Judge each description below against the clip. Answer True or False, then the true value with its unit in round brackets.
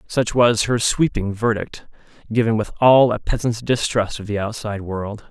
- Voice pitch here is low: True (110 Hz)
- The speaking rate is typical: True (170 wpm)